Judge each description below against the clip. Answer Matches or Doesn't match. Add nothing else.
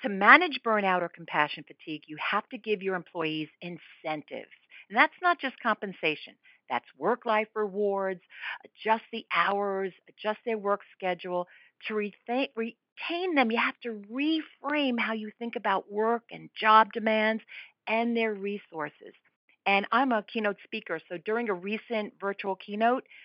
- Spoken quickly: Doesn't match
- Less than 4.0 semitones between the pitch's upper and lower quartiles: Matches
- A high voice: Matches